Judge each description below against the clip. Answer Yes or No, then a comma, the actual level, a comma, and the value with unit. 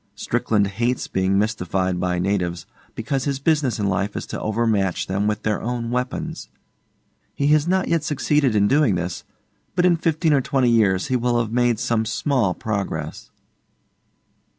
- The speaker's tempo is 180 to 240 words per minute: No, average, 165 wpm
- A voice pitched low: Yes, low, 115 Hz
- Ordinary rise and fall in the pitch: No, wide, 5.7 semitones